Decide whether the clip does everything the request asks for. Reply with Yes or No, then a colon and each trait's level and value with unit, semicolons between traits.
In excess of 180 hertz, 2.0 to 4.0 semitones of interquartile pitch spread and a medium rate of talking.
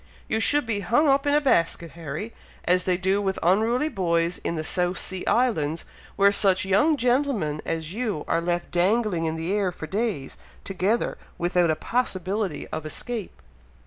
No: high, 190 Hz; average, 5.3 semitones; average, 175 wpm